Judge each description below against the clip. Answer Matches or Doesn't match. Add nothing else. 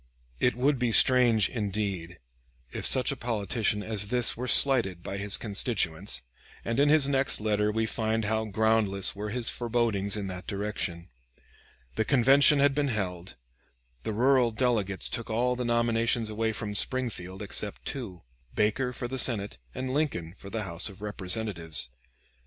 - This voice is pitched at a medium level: Doesn't match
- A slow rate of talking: Doesn't match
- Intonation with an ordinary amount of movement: Matches